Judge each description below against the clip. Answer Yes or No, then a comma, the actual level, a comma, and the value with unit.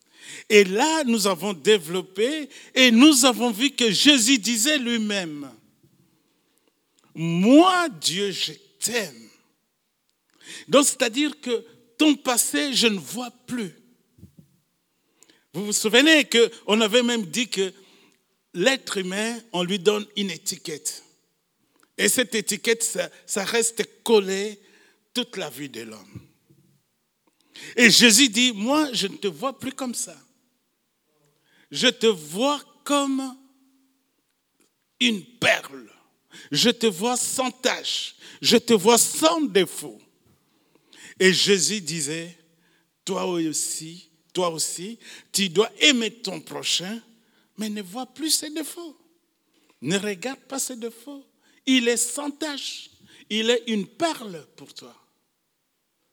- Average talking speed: No, slow, 125 wpm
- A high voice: Yes, high, 230 Hz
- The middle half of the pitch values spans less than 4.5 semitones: No, average, 5.3 semitones